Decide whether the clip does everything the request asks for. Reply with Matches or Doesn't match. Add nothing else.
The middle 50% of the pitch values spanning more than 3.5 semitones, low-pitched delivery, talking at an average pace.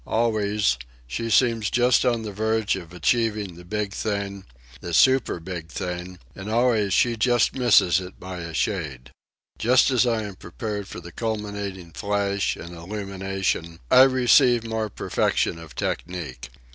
Matches